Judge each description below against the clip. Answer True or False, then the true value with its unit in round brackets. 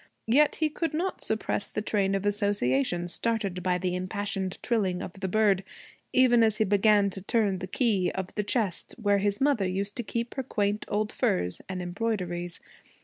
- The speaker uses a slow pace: False (185 wpm)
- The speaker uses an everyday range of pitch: True (3.1 semitones)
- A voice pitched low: False (205 Hz)